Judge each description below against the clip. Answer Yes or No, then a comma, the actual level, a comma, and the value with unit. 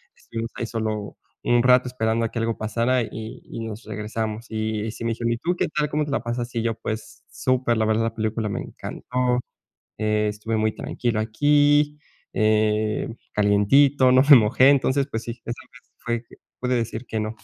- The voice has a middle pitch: No, low, 115 Hz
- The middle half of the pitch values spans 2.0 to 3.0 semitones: Yes, narrow, 2.6 semitones